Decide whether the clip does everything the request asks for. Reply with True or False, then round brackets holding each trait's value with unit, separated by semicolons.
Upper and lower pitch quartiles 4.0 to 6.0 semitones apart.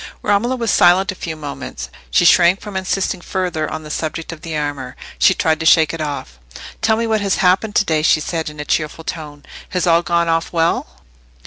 False (3.4 semitones)